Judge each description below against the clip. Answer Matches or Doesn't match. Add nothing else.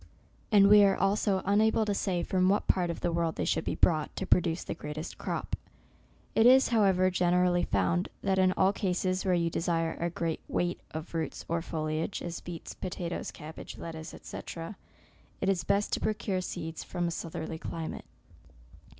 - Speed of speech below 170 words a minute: Doesn't match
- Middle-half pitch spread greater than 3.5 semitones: Doesn't match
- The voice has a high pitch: Doesn't match